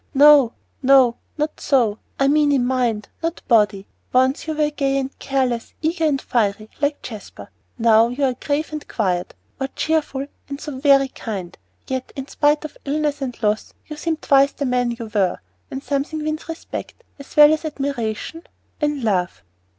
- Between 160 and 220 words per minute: Yes, average, 175 wpm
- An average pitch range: Yes, average, 4.2 semitones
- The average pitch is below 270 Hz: No, very high, 275 Hz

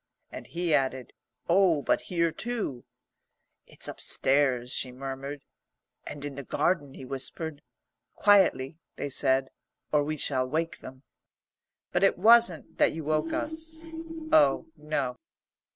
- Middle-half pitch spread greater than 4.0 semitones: Yes, average, 4.8 semitones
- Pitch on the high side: No, medium, 150 Hz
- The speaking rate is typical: No, slow, 130 wpm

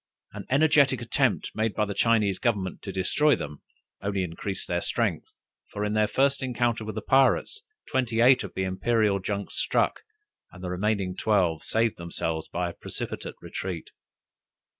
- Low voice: Yes, low, 105 Hz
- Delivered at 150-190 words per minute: Yes, average, 160 wpm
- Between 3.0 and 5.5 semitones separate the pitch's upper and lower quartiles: Yes, average, 4.2 semitones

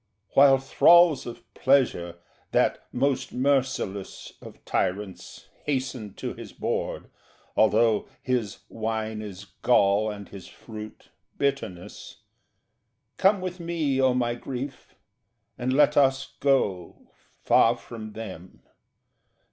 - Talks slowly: Yes, slow, 110 wpm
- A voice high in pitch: No, low, 120 Hz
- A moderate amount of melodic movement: Yes, average, 4.6 semitones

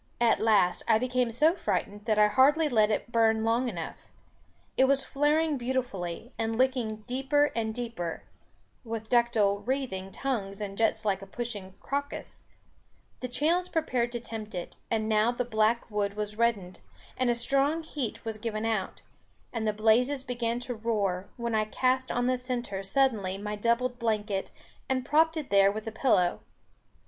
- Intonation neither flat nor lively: Yes, average, 3.3 semitones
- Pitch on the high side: Yes, high, 230 Hz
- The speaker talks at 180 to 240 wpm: No, average, 170 wpm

